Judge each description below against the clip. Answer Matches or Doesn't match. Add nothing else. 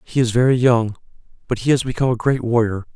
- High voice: Doesn't match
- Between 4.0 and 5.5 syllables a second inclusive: Doesn't match